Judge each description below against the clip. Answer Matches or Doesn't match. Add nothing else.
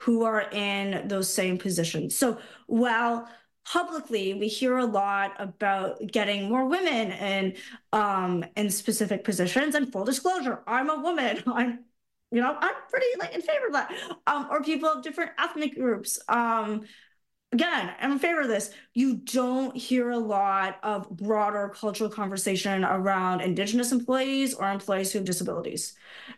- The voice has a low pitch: Doesn't match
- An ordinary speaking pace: Matches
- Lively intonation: Doesn't match